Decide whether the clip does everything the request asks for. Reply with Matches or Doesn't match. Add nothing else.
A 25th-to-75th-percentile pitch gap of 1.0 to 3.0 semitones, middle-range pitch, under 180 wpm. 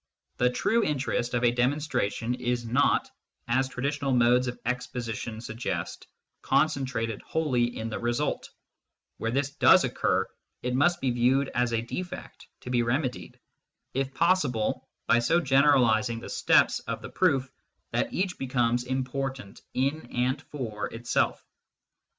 Doesn't match